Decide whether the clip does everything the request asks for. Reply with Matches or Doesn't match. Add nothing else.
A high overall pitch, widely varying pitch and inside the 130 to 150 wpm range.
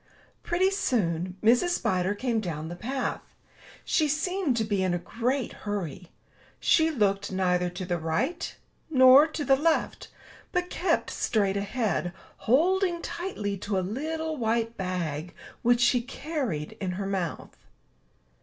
Matches